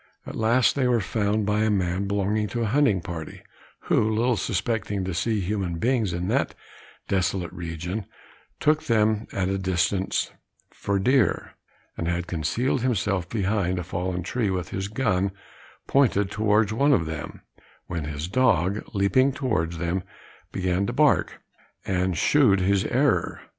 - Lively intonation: No, average, 3.7 semitones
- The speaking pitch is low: Yes, low, 100 Hz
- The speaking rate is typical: Yes, average, 155 wpm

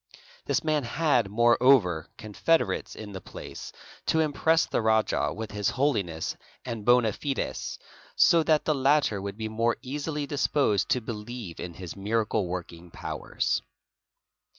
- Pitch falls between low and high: No, low, 115 Hz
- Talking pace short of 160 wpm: Yes, average, 150 wpm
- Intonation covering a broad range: Yes, wide, 5.9 semitones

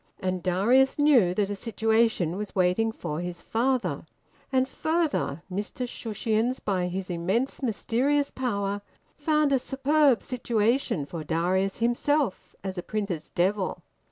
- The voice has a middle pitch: No, high, 215 Hz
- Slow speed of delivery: Yes, slow, 130 wpm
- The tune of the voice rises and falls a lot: Yes, wide, 5.8 semitones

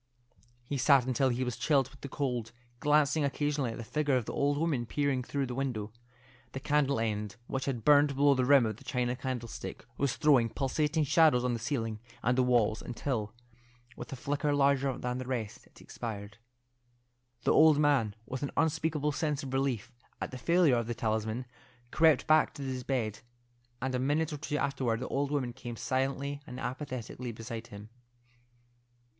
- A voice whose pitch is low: Yes, low, 130 Hz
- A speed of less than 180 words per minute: No, average, 185 wpm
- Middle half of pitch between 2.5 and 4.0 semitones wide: Yes, average, 3.2 semitones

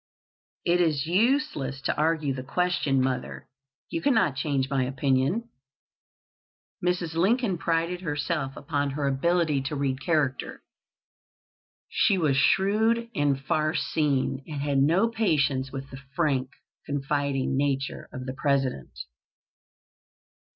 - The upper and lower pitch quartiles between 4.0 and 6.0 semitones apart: Yes, average, 4.3 semitones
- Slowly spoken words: Yes, slow, 120 wpm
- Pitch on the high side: No, medium, 145 Hz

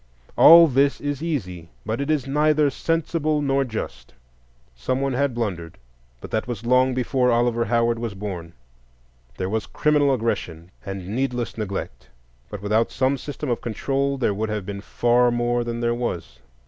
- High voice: No, low, 120 Hz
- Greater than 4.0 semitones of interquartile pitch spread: Yes, average, 4.8 semitones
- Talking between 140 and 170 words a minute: Yes, average, 160 wpm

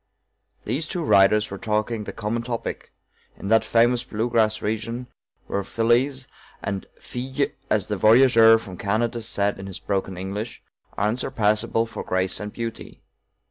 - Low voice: Yes, low, 110 Hz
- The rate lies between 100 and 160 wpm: Yes, average, 155 wpm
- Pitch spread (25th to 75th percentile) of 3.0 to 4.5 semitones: No, narrow, 2.5 semitones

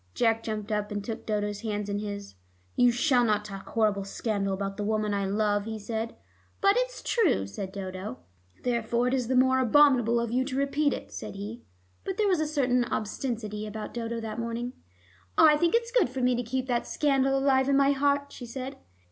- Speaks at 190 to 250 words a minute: Yes, fast, 205 wpm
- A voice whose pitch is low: No, high, 235 Hz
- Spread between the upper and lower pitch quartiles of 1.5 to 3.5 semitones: No, average, 4.2 semitones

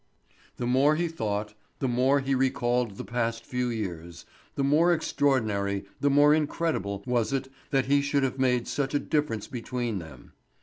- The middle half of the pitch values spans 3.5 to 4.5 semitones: Yes, average, 4.2 semitones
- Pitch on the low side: Yes, low, 125 Hz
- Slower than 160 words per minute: No, average, 170 wpm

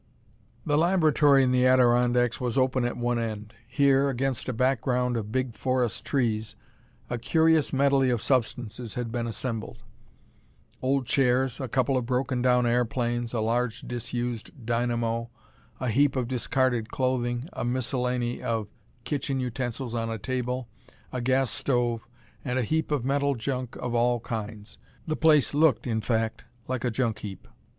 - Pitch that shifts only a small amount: Yes, narrow, 2.0 semitones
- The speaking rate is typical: Yes, average, 155 wpm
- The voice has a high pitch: No, low, 125 Hz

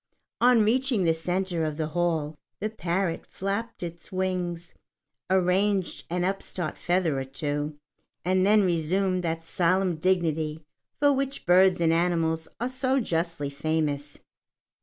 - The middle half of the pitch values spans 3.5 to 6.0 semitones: No, average, 3.0 semitones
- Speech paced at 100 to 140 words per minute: Yes, slow, 135 wpm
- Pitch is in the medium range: Yes, medium, 175 Hz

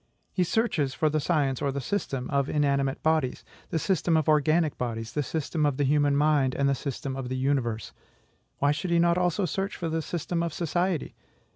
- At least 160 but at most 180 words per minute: No, fast, 205 wpm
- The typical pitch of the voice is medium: Yes, medium, 150 Hz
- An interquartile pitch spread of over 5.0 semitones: No, average, 3.5 semitones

